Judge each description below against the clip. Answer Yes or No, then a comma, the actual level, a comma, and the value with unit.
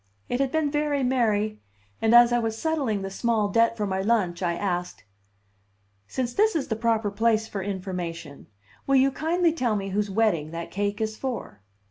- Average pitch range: Yes, average, 4.5 semitones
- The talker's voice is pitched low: No, high, 220 Hz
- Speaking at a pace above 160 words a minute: Yes, average, 185 wpm